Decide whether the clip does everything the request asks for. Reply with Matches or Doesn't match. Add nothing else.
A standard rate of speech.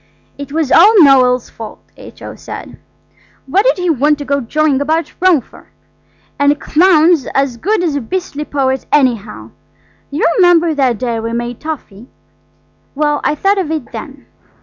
Matches